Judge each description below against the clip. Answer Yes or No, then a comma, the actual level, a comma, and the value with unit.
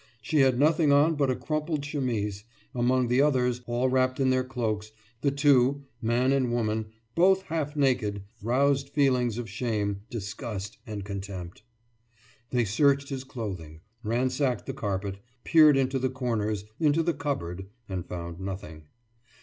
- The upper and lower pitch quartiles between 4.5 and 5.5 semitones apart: Yes, average, 4.9 semitones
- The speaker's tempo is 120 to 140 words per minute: No, average, 150 wpm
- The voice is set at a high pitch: No, low, 125 Hz